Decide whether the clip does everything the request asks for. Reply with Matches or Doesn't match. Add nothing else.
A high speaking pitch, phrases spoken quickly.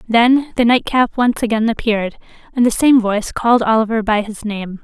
Doesn't match